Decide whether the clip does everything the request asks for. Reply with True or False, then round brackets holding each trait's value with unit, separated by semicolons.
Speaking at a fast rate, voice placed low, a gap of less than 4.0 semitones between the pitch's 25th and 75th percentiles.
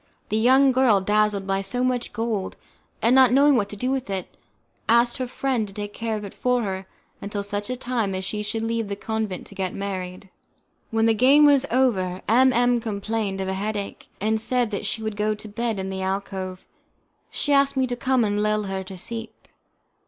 False (210 wpm; 215 Hz; 3.6 semitones)